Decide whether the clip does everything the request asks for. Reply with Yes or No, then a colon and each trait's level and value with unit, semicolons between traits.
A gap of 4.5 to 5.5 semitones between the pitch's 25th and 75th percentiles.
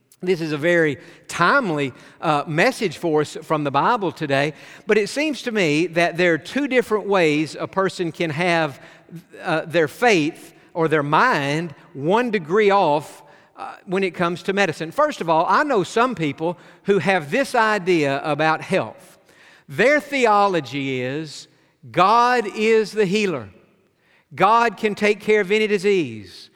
Yes: average, 5.1 semitones